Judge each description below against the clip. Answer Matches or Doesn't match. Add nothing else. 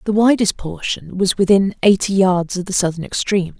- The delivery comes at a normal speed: Matches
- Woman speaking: Matches